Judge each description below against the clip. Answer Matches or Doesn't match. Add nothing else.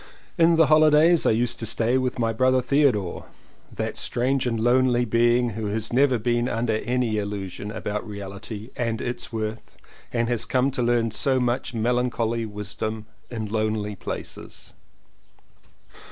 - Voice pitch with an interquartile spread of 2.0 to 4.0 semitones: Matches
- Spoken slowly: Doesn't match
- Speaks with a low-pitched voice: Matches